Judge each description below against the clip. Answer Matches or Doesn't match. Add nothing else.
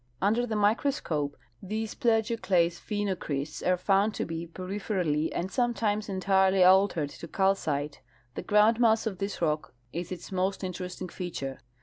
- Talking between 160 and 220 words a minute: Doesn't match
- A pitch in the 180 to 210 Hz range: Matches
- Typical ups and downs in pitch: Matches